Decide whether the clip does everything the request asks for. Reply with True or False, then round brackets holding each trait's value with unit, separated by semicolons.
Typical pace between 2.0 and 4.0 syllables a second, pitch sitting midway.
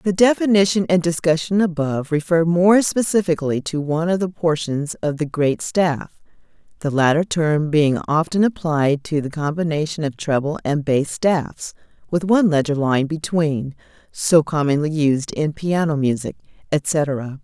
False (4.2 syllables/s; 160 Hz)